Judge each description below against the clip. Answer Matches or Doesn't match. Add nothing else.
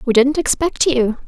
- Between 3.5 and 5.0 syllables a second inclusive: Matches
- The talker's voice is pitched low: Doesn't match